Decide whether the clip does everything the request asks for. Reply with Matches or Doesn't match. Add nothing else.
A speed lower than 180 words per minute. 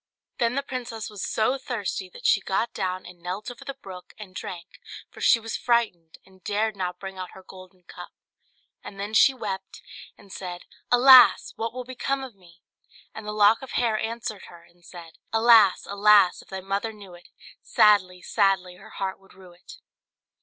Doesn't match